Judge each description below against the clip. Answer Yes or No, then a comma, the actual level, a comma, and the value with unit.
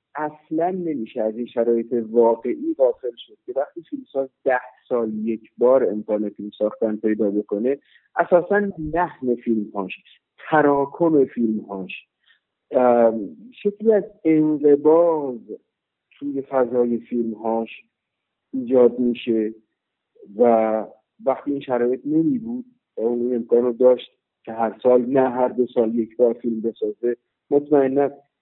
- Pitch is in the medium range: No, low, 125 Hz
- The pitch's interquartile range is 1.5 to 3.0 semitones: No, average, 5.3 semitones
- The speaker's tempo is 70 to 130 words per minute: Yes, average, 120 wpm